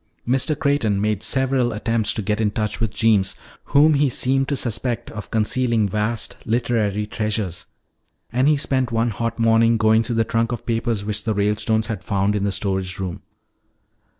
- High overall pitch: No, low, 115 Hz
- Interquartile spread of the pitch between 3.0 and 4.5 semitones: No, narrow, 2.4 semitones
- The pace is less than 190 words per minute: Yes, average, 180 wpm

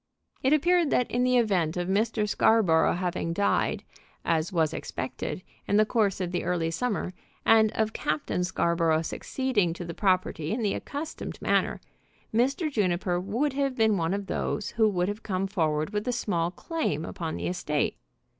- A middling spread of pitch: Yes, average, 5.0 semitones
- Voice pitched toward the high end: Yes, high, 195 Hz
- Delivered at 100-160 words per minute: No, average, 175 wpm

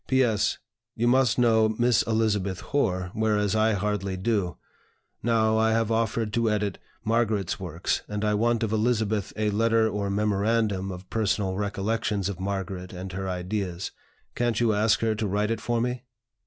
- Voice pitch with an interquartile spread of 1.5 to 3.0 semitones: Yes, narrow, 2.5 semitones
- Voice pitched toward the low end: Yes, low, 105 Hz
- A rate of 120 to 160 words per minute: No, average, 170 wpm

